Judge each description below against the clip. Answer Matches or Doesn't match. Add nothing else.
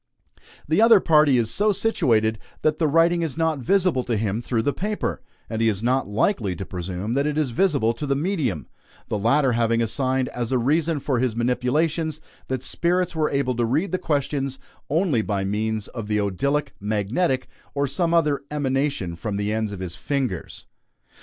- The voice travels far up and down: Matches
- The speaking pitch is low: Matches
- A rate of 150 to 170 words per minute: Doesn't match